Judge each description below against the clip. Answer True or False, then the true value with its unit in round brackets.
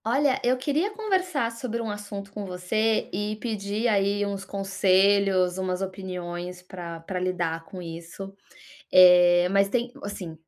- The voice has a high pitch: True (195 Hz)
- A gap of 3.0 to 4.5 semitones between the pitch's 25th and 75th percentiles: True (3.3 semitones)